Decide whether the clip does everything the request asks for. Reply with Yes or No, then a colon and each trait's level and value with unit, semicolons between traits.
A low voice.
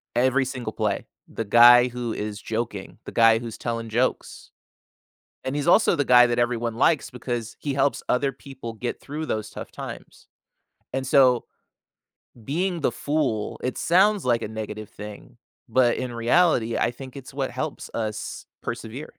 Yes: low, 120 Hz